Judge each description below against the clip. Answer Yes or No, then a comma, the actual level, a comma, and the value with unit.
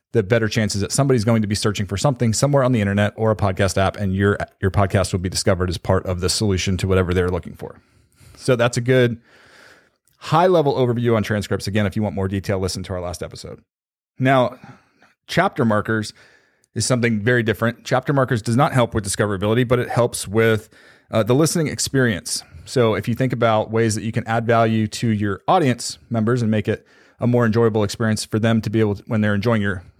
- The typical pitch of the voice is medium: No, low, 110 Hz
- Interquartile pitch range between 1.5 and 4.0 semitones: Yes, average, 2.8 semitones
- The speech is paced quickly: Yes, fast, 220 wpm